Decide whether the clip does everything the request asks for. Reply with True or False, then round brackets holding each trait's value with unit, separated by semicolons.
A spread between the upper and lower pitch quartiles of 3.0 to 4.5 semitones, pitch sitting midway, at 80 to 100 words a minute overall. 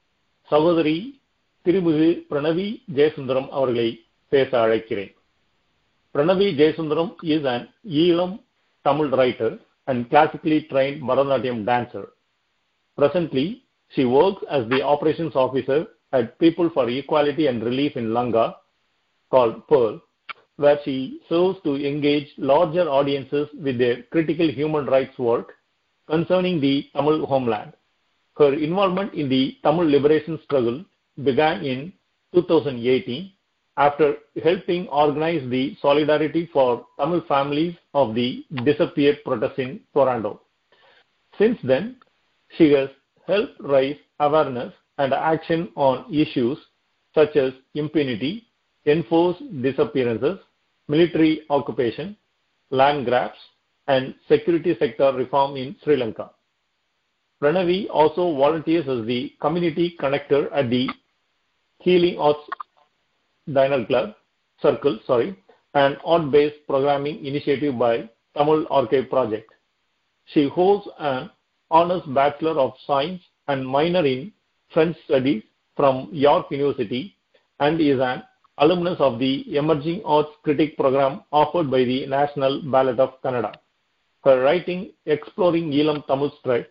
False (3.5 semitones; 145 Hz; 110 wpm)